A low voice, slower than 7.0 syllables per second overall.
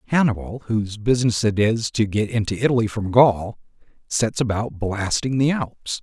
Yes: low, 110 Hz; 5.0 syllables/s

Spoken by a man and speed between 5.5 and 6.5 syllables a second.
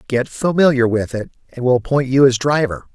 Yes: male; 5.6 syllables/s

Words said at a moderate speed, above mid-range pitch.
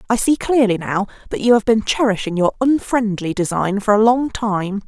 Yes: average, 195 wpm; high, 215 Hz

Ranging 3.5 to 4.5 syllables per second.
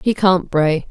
Yes: 3.8 syllables/s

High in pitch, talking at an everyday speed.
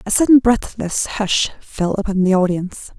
Yes: high, 205 Hz; average, 160 wpm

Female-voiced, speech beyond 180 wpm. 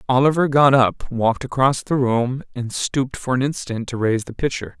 No: male; average, 200 wpm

